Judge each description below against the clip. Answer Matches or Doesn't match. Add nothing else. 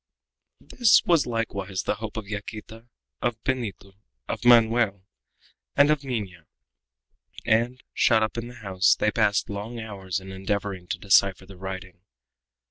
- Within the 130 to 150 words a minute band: Matches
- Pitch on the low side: Matches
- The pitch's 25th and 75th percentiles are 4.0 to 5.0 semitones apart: Doesn't match